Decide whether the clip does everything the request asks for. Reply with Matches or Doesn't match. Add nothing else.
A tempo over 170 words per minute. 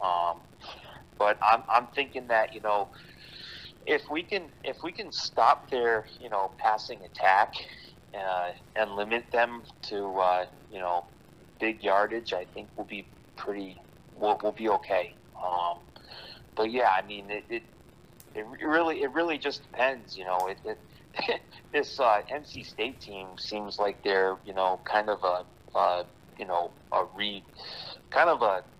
Doesn't match